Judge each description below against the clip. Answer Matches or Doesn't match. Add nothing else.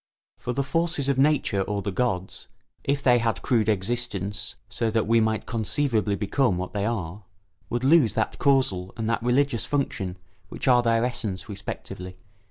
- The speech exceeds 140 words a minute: Matches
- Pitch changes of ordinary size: Matches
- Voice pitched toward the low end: Matches